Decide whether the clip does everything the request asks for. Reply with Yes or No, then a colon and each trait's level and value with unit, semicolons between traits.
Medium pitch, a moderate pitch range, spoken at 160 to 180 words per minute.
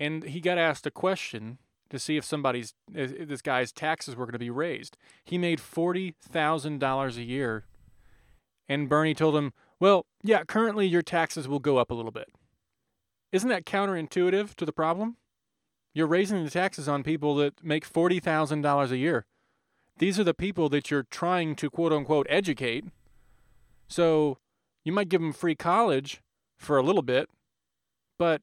Yes: medium, 155 Hz; average, 4.0 semitones; average, 165 wpm